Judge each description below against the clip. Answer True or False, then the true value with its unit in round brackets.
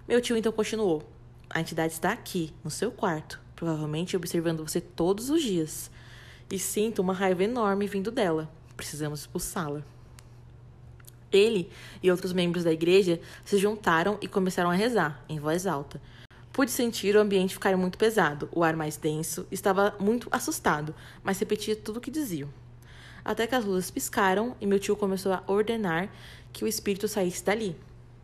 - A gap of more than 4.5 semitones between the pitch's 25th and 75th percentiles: True (4.9 semitones)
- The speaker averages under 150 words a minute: False (165 wpm)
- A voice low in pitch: False (185 Hz)